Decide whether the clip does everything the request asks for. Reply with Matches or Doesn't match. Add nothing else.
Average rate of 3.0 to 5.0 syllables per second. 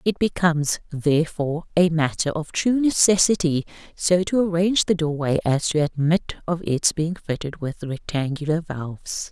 Matches